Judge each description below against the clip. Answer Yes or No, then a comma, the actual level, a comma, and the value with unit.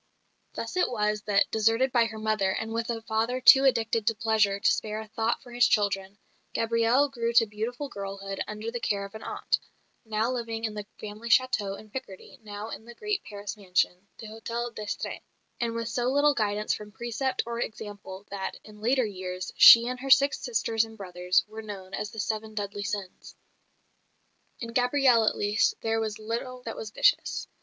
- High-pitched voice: Yes, high, 220 Hz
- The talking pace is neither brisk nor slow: Yes, average, 190 wpm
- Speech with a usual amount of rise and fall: No, narrow, 2.3 semitones